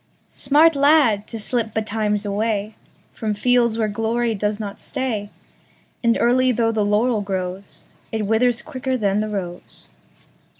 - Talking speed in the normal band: No, slow, 125 wpm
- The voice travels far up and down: No, average, 2.8 semitones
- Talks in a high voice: Yes, high, 220 Hz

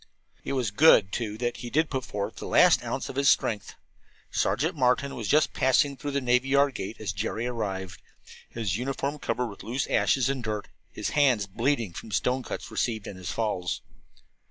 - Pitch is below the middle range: Yes, low, 120 Hz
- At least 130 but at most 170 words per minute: No, average, 195 wpm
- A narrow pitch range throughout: No, average, 4.6 semitones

